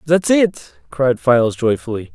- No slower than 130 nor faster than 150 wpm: Yes, average, 140 wpm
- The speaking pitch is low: Yes, low, 130 Hz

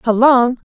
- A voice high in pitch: Yes, high, 245 Hz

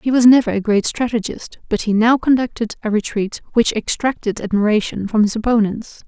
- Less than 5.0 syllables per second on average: No, 5.4 syllables/s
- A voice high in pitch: Yes, high, 225 Hz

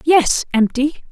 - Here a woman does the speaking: Yes, female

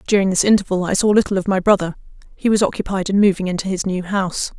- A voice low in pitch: No, high, 190 Hz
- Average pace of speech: No, fast, 235 wpm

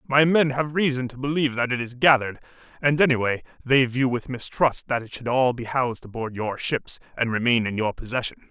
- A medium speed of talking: No, fast, 210 wpm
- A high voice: No, low, 125 Hz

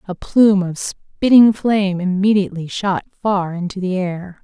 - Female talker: Yes, female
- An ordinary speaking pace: Yes, average, 150 wpm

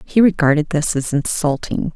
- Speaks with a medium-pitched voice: Yes, medium, 160 Hz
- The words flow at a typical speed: Yes, average, 155 wpm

